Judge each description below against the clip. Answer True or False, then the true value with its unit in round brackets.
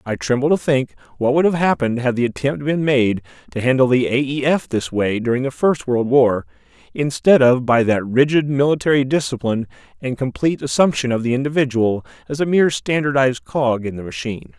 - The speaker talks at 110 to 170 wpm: False (195 wpm)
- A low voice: True (130 Hz)